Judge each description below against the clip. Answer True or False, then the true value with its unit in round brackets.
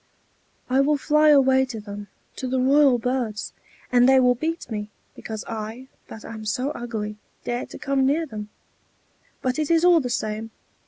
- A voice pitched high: True (250 Hz)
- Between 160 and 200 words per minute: True (175 wpm)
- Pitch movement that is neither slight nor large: True (3.9 semitones)